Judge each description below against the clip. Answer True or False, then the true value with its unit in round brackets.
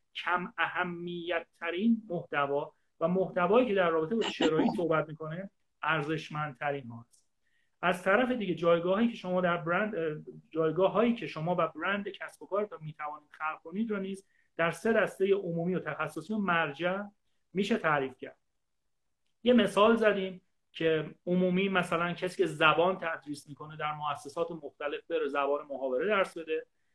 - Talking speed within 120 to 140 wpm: False (155 wpm)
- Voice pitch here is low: False (170 Hz)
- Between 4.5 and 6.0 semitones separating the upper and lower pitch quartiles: False (3.7 semitones)